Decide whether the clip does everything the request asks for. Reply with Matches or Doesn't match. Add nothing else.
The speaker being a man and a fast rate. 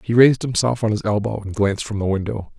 Matches